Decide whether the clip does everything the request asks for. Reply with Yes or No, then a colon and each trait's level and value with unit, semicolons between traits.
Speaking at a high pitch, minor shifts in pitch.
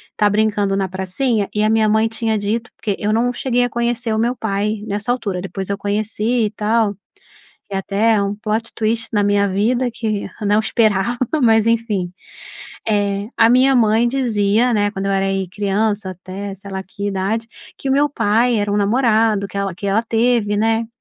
Yes: high, 215 Hz; narrow, 2.3 semitones